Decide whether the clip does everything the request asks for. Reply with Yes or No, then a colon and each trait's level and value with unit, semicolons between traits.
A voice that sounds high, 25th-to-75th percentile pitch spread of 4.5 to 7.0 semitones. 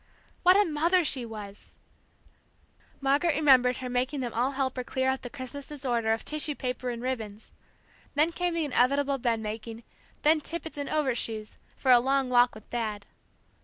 No: very high, 260 Hz; average, 3.4 semitones